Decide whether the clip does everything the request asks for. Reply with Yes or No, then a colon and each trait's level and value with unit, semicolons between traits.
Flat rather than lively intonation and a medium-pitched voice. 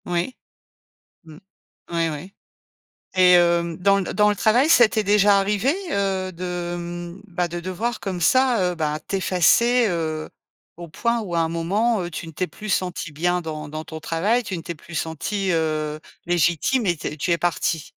No: average, 3.4 semitones; medium, 175 Hz